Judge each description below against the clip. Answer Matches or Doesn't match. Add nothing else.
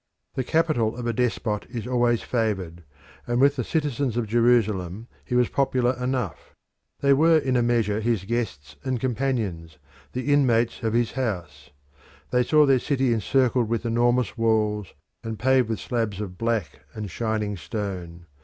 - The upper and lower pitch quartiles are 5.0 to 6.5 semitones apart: Doesn't match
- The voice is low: Matches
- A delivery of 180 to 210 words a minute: Doesn't match